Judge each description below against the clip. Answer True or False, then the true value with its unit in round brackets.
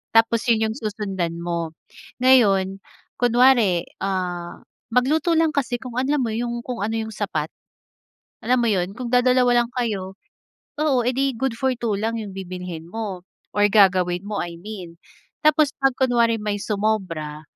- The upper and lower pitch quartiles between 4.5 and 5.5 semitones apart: True (4.9 semitones)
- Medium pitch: False (220 Hz)